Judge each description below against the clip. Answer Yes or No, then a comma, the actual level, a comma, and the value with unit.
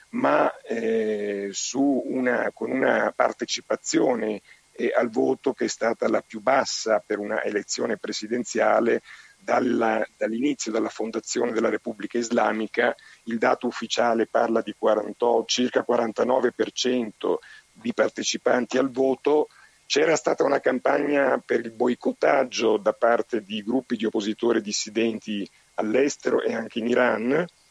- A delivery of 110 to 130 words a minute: Yes, average, 125 wpm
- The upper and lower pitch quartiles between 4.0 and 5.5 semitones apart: No, narrow, 2.6 semitones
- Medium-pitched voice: No, low, 115 Hz